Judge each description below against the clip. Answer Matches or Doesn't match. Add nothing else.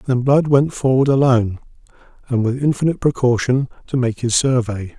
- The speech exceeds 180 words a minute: Doesn't match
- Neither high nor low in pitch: Doesn't match